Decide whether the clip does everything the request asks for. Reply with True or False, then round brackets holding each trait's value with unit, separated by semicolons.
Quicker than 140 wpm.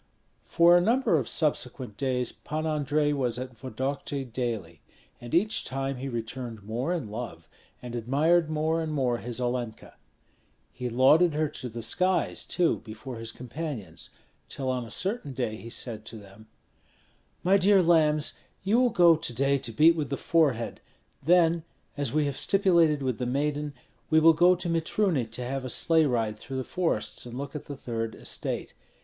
True (180 wpm)